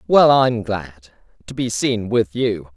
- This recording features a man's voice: Yes, male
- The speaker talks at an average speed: Yes, average, 150 wpm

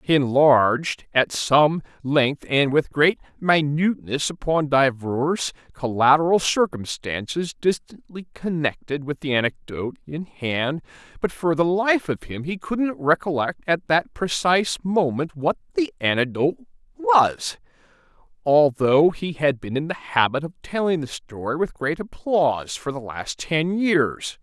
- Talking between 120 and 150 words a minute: Yes, average, 140 wpm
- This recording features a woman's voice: No, male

